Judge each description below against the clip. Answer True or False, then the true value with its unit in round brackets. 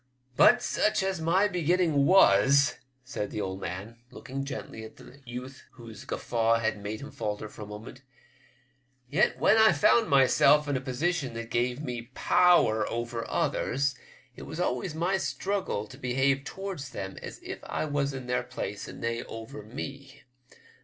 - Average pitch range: True (4.6 semitones)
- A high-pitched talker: False (130 Hz)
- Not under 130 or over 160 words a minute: False (175 wpm)